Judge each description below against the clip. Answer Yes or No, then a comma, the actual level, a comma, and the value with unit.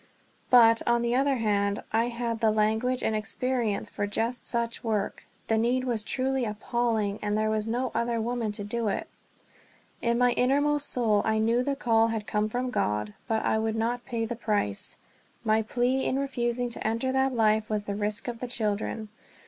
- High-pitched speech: Yes, high, 230 Hz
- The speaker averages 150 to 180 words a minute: No, average, 195 wpm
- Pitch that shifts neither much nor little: No, narrow, 2.3 semitones